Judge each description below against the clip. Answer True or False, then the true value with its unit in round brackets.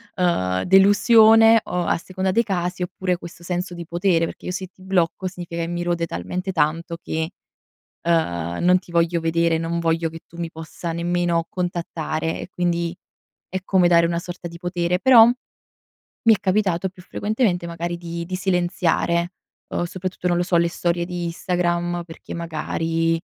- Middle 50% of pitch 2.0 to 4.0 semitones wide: False (1.4 semitones)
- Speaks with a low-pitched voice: False (175 Hz)